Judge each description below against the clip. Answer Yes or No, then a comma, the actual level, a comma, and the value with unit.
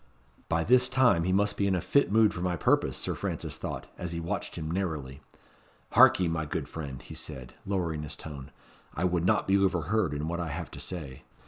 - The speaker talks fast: Yes, fast, 220 wpm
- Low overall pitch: Yes, very low, 85 Hz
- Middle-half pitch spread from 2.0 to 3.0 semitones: No, average, 3.7 semitones